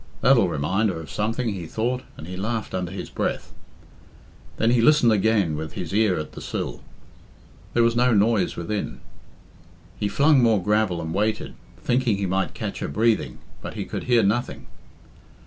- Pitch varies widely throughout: No, average, 4.2 semitones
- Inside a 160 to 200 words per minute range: Yes, average, 175 wpm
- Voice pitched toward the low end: Yes, low, 105 Hz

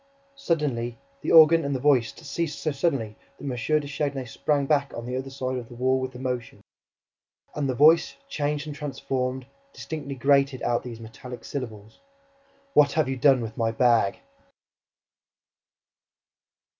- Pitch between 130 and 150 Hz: Yes, low, 135 Hz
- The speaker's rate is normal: Yes, average, 155 wpm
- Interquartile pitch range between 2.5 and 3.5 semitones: Yes, average, 2.9 semitones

